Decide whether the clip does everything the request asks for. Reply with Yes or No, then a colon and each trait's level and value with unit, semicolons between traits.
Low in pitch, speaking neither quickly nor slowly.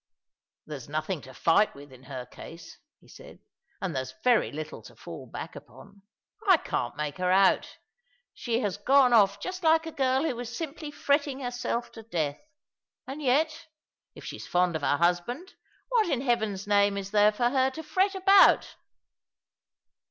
No: high, 225 Hz; average, 175 wpm